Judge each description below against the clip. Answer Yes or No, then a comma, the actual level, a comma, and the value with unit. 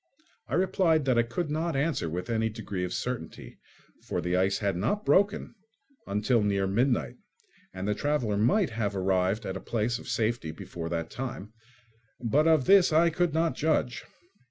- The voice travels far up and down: Yes, wide, 7.9 semitones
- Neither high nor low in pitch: No, low, 115 Hz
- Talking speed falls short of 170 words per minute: No, average, 175 wpm